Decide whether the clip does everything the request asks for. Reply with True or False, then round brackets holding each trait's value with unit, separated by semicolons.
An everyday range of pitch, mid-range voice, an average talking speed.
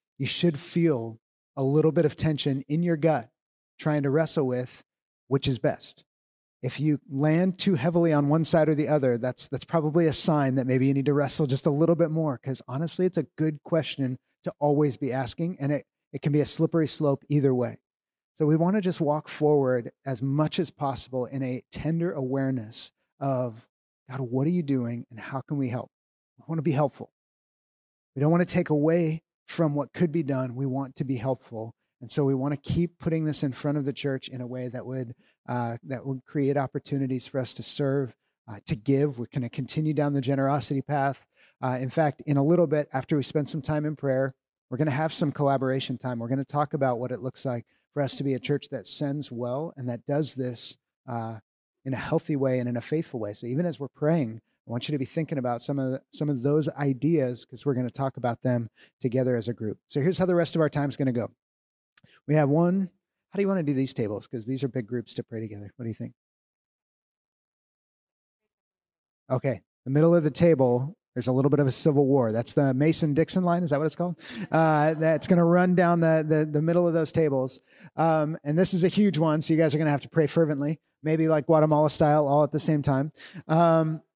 False (3.5 semitones; 145 Hz; 235 wpm)